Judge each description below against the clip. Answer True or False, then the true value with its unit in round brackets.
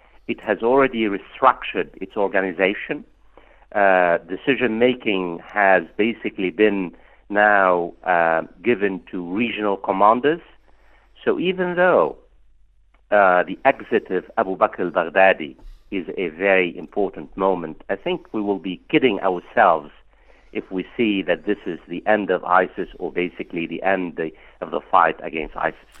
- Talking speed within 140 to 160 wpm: True (145 wpm)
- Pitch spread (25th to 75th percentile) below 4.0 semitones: True (2.8 semitones)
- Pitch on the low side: True (95 Hz)